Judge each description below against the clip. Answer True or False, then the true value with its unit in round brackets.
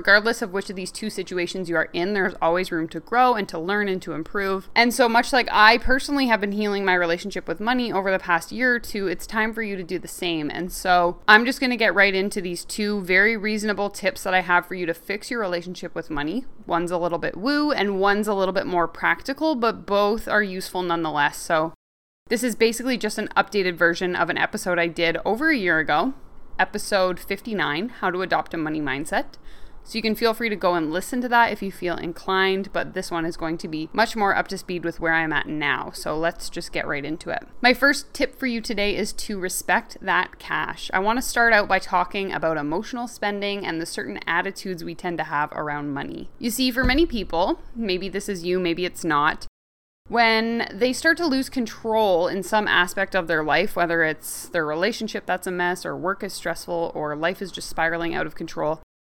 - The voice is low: False (190 Hz)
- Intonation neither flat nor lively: True (4.3 semitones)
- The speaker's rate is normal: False (230 wpm)